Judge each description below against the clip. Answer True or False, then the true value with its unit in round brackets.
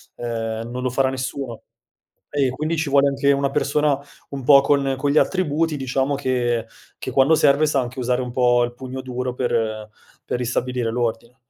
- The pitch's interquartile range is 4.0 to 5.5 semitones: False (2.4 semitones)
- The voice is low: True (130 Hz)